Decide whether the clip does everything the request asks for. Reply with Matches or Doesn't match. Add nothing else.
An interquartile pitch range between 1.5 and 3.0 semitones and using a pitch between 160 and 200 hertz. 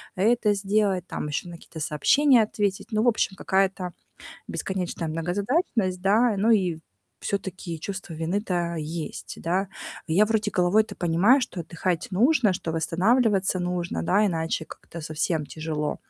Doesn't match